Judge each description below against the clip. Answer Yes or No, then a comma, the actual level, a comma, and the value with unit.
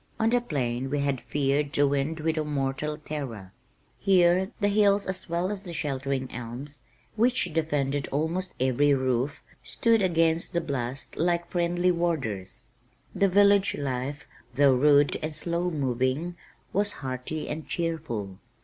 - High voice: No, medium, 150 Hz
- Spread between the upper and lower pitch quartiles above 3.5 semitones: Yes, average, 4.4 semitones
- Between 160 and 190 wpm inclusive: No, average, 145 wpm